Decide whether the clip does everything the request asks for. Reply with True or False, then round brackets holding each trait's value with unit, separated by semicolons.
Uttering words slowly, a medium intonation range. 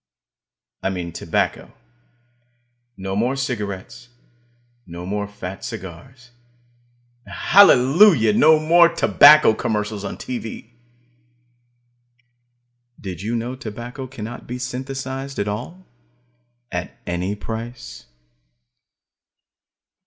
True (90 wpm; 4.7 semitones)